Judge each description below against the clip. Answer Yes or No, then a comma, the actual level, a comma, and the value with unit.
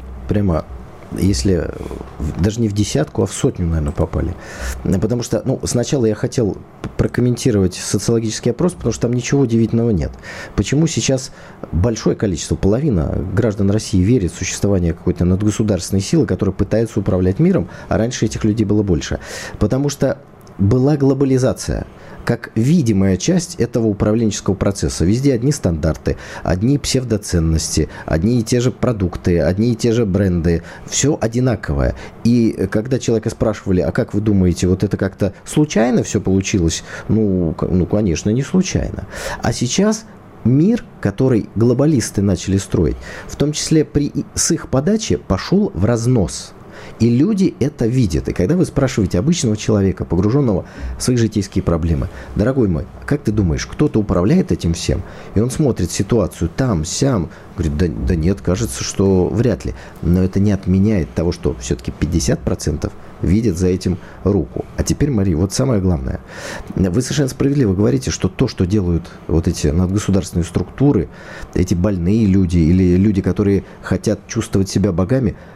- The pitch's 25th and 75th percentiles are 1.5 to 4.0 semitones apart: No, average, 5.0 semitones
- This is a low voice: Yes, low, 105 Hz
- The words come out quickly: No, average, 150 wpm